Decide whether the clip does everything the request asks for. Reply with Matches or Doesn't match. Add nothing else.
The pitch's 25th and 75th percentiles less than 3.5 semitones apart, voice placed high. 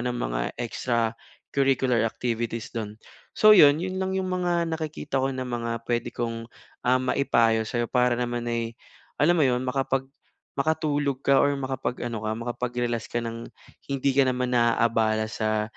Doesn't match